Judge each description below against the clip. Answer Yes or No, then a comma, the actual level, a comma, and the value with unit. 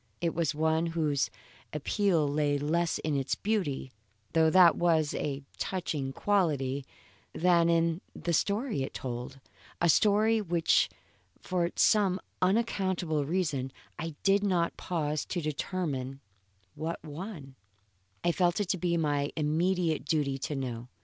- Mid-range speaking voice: Yes, medium, 165 Hz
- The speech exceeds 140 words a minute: No, slow, 135 wpm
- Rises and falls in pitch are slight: No, average, 3.9 semitones